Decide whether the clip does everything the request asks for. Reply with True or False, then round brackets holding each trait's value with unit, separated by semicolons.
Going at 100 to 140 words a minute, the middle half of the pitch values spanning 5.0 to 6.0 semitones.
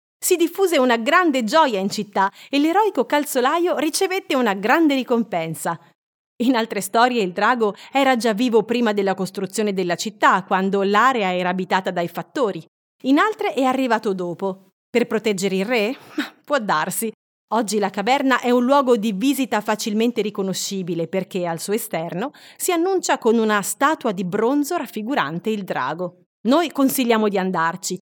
False (155 wpm; 5.5 semitones)